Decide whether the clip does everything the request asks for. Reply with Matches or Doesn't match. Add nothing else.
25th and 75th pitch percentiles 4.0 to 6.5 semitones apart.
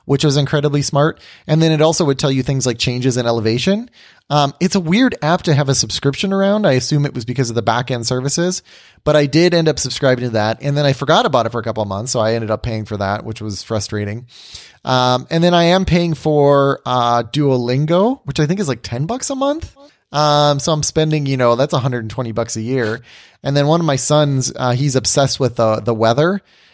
Matches